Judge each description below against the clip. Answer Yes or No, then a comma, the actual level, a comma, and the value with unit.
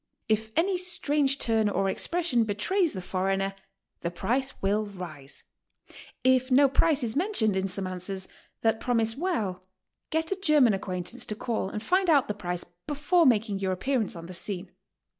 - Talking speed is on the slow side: No, average, 180 wpm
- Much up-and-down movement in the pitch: Yes, wide, 6.8 semitones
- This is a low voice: No, high, 220 Hz